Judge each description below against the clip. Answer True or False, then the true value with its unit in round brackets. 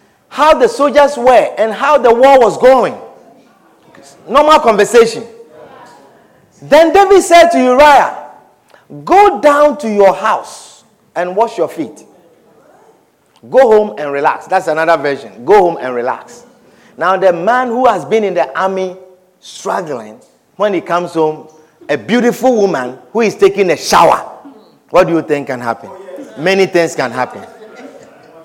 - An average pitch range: False (7.5 semitones)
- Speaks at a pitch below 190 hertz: False (220 Hz)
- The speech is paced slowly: False (145 wpm)